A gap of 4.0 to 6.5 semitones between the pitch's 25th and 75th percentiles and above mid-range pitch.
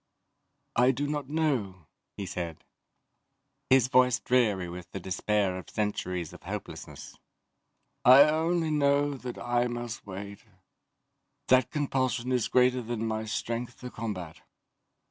No: average, 4.5 semitones; low, 120 Hz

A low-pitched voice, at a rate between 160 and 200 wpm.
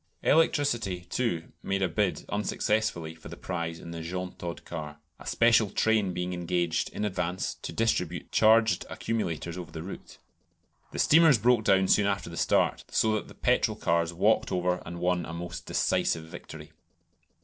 Yes: very low, 90 Hz; average, 165 wpm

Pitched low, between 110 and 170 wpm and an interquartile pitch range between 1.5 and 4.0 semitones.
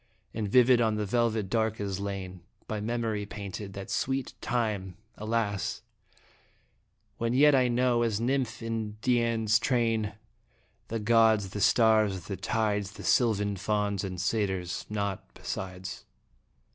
Yes: low, 110 Hz; slow, 135 wpm; narrow, 2.6 semitones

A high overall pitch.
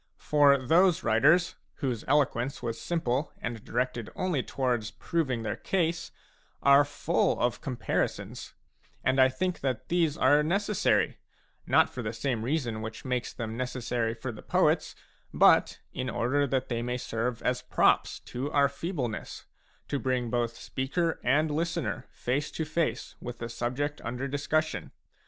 No: low, 130 Hz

